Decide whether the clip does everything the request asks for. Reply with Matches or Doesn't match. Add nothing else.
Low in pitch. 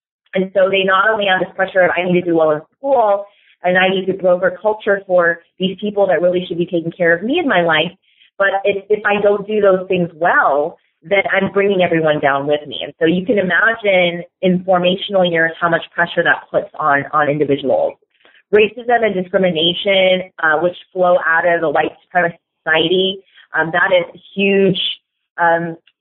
Doesn't match